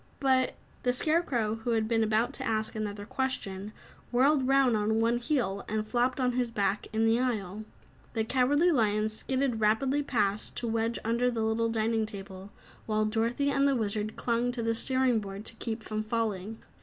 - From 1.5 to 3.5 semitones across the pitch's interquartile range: Yes, average, 2.7 semitones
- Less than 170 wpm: No, average, 185 wpm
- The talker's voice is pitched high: Yes, high, 225 Hz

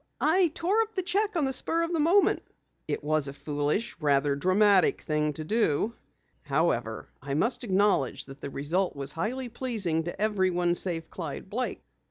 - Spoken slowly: No, average, 170 wpm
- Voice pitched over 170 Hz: Yes, medium, 185 Hz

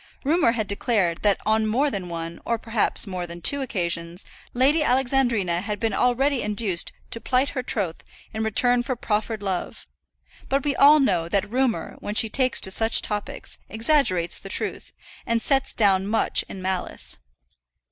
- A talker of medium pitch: No, high, 220 Hz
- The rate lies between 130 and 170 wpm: Yes, average, 165 wpm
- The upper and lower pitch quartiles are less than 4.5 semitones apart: No, average, 5.0 semitones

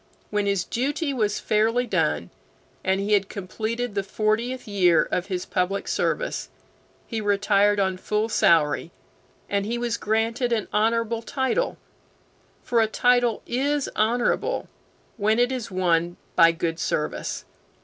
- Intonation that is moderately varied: Yes, average, 3.4 semitones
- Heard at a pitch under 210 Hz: No, high, 215 Hz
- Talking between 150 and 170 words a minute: No, average, 140 wpm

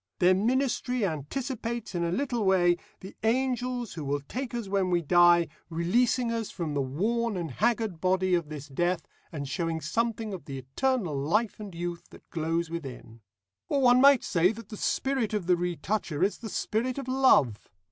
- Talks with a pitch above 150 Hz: Yes, high, 190 Hz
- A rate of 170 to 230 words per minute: Yes, average, 180 wpm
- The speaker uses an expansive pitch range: Yes, wide, 6.0 semitones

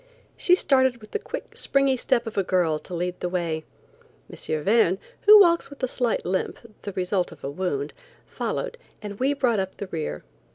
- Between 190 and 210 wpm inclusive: Yes, average, 195 wpm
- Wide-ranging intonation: Yes, wide, 6.8 semitones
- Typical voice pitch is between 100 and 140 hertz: No, high, 200 Hz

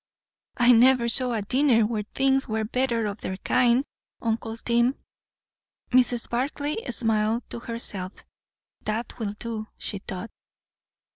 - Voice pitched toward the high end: Yes, high, 235 Hz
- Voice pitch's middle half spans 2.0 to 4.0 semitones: Yes, narrow, 2.6 semitones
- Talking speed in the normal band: No, slow, 130 wpm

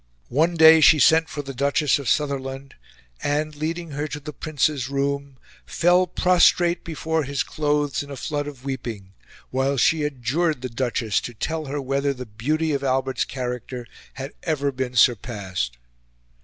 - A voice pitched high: No, medium, 140 Hz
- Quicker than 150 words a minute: Yes, average, 160 wpm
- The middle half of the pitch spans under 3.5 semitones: Yes, average, 3.1 semitones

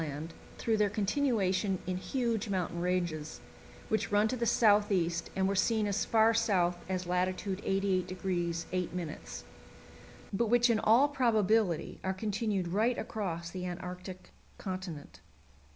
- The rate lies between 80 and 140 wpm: Yes, slow, 135 wpm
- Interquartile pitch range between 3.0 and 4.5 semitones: Yes, average, 3.4 semitones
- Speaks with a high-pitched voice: Yes, high, 195 Hz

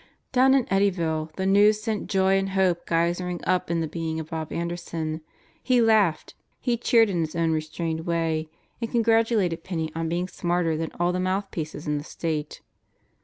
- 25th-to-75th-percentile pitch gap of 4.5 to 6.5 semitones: No, average, 3.4 semitones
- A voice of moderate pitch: Yes, medium, 175 Hz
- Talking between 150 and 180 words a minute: Yes, average, 175 wpm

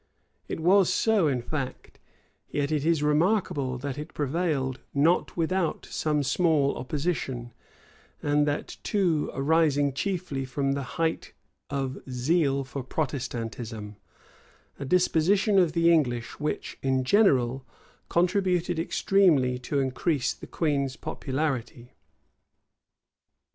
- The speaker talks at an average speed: No, slow, 110 wpm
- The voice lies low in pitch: No, medium, 145 Hz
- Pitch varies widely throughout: No, average, 4.1 semitones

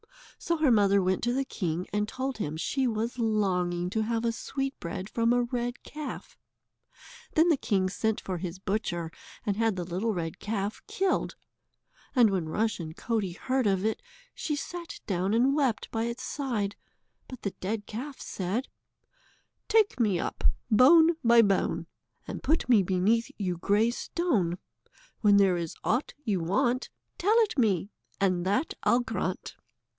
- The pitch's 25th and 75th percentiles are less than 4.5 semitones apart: No, average, 5.0 semitones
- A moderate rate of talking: Yes, average, 160 wpm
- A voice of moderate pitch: No, high, 220 Hz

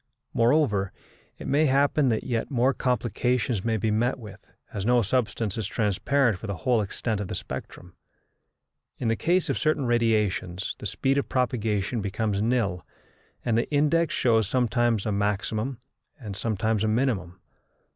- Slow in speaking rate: No, average, 155 wpm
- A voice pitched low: Yes, low, 115 Hz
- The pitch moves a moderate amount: Yes, average, 3.5 semitones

